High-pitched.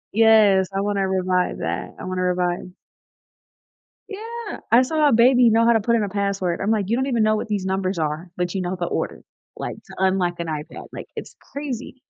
Yes: high, 200 Hz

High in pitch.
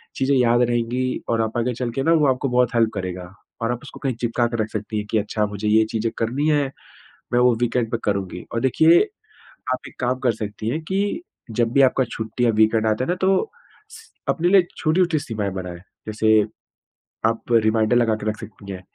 No: low, 115 Hz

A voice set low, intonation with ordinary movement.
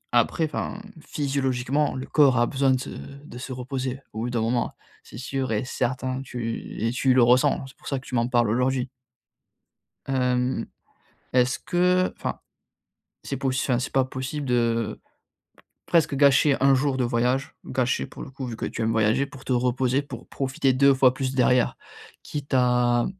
No: low, 130 Hz; narrow, 1.8 semitones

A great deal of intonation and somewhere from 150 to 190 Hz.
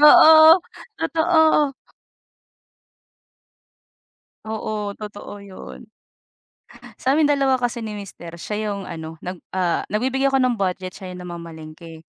No: wide, 6.7 semitones; high, 210 Hz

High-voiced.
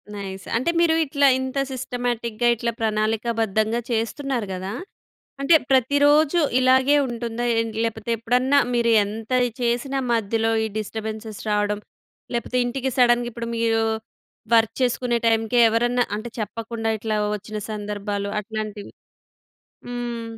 Yes: high, 230 Hz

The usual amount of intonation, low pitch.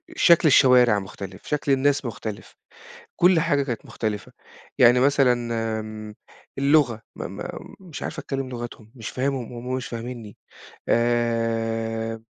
Yes: average, 3.3 semitones; low, 120 Hz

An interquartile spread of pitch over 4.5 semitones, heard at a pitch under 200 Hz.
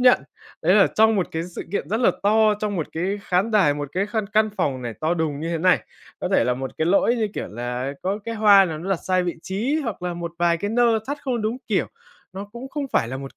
Yes: average, 5.2 semitones; high, 190 Hz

